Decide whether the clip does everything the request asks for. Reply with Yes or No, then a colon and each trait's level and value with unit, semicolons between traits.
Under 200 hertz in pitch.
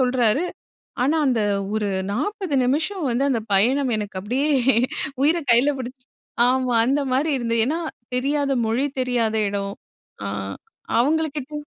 No: very high, 255 Hz